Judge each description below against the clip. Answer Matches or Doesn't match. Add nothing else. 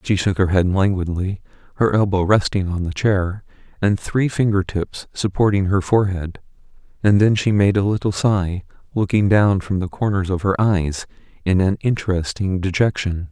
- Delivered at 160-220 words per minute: Matches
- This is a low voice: Matches